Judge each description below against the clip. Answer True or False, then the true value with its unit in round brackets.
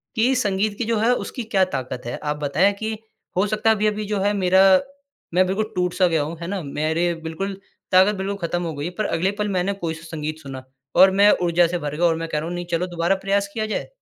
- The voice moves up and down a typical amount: True (3.7 semitones)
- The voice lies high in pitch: False (180 Hz)